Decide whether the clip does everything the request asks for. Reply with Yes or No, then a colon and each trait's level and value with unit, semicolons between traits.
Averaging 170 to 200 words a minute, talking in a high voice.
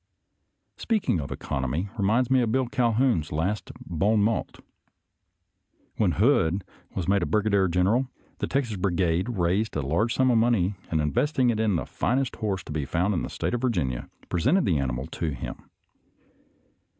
No: average, 175 wpm; low, 100 Hz